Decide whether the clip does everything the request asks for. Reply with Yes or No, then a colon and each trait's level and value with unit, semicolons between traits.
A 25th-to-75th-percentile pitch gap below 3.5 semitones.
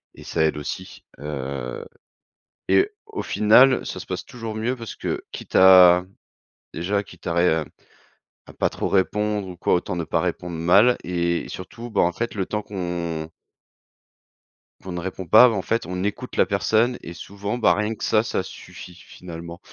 No: average, 3.8 semitones